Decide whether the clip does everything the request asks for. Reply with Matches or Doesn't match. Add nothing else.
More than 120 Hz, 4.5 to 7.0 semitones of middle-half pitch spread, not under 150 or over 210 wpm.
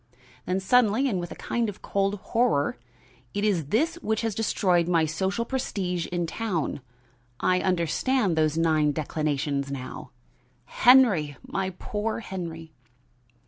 Doesn't match